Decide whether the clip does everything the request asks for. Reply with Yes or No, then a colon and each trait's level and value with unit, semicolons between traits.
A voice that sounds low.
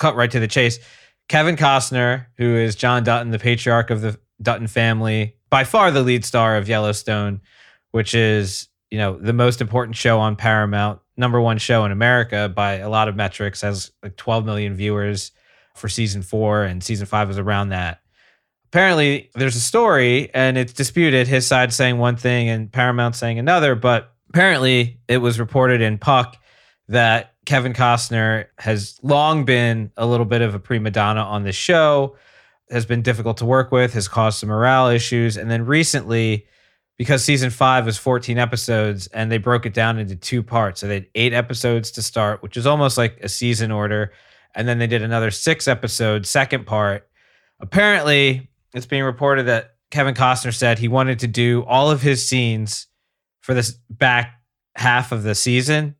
Yes: low, 120 Hz